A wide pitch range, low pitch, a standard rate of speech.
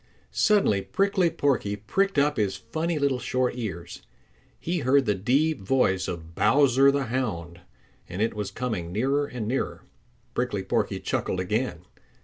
Yes: wide, 6.4 semitones; low, 125 Hz; average, 145 wpm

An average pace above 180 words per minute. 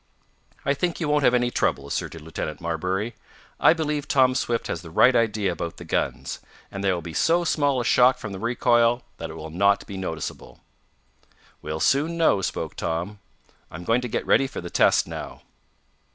Yes: average, 195 wpm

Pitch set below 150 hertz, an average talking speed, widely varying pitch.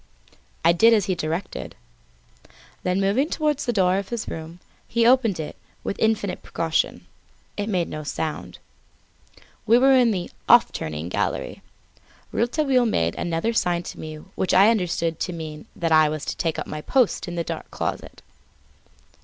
No: medium, 180 Hz; average, 165 wpm; wide, 5.8 semitones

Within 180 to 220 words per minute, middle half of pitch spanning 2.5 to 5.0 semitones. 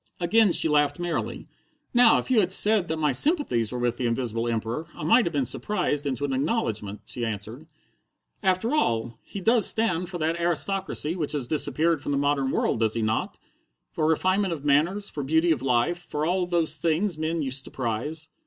No: average, 200 wpm; wide, 5.4 semitones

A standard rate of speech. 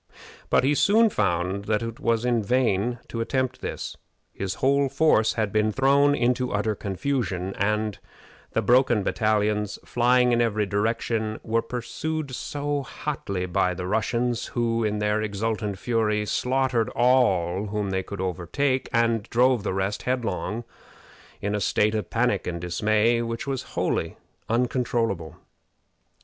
Yes: average, 145 wpm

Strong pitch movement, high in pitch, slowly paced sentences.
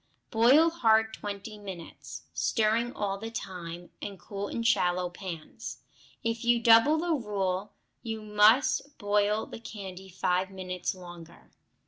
No: average, 3.6 semitones; high, 205 Hz; slow, 130 wpm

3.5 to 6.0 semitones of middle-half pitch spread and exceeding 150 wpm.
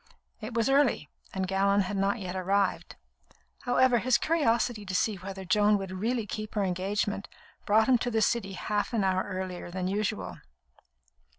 No: average, 3.1 semitones; average, 170 wpm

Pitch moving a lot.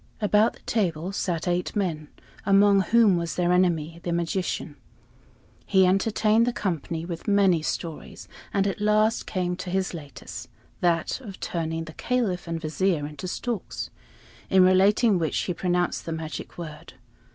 No: average, 3.2 semitones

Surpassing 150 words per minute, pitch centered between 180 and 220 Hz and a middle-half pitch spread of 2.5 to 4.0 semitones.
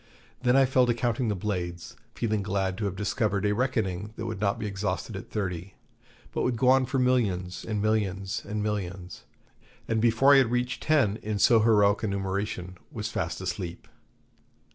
No: average, 185 wpm; low, 105 Hz; average, 3.3 semitones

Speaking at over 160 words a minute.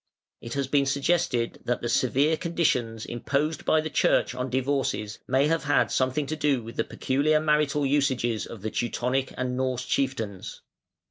Yes: average, 170 wpm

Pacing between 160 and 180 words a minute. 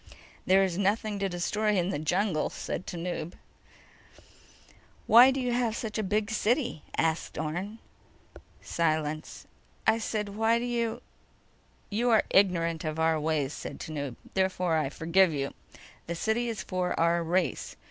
No: average, 145 wpm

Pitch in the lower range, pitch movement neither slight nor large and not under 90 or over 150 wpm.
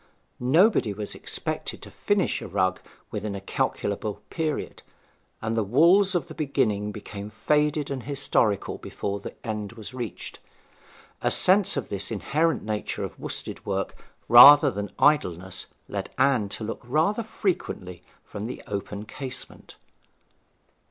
No: low, 115 Hz; wide, 6.5 semitones; average, 140 wpm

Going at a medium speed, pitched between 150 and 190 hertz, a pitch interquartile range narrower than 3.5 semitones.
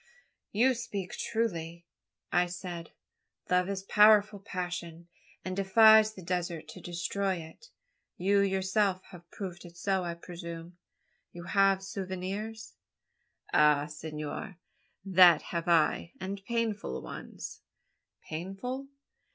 No: slow, 120 wpm; medium, 185 Hz; narrow, 2.6 semitones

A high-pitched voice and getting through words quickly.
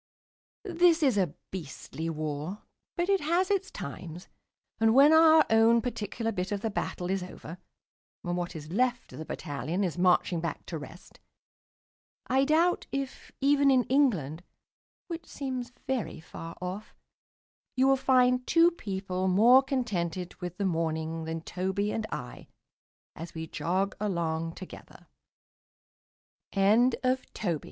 No: high, 200 Hz; slow, 135 wpm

